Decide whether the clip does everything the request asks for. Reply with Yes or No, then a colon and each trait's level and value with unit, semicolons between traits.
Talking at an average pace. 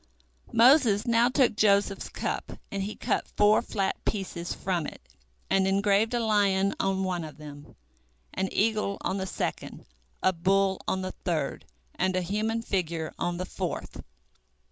Yes: average, 155 wpm